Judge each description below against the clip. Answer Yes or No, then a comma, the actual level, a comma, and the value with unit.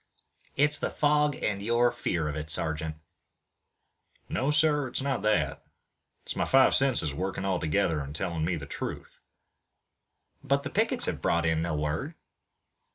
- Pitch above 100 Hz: No, very low, 90 Hz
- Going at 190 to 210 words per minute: No, average, 160 wpm